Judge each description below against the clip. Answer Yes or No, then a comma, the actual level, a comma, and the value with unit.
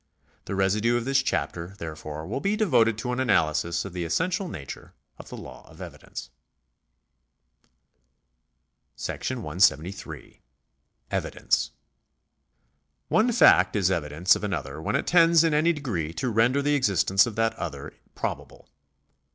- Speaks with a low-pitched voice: Yes, low, 105 Hz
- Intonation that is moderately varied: No, wide, 8.7 semitones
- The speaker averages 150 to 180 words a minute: No, slow, 135 wpm